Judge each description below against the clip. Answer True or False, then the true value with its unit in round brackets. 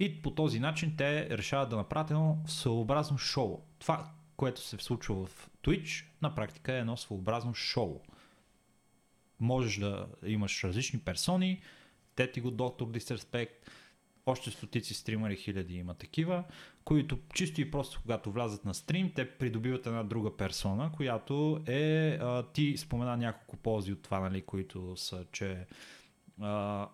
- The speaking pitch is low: True (120 Hz)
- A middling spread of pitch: False (5.9 semitones)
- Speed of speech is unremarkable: True (145 wpm)